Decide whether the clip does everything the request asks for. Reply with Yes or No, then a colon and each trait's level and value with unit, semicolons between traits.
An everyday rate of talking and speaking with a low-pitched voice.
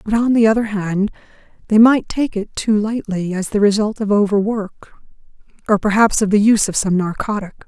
No: average, 190 wpm; high, 210 Hz